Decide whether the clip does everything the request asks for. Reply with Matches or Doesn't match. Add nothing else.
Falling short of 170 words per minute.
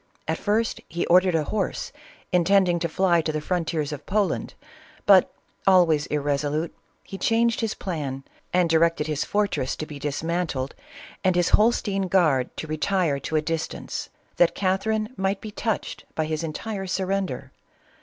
Matches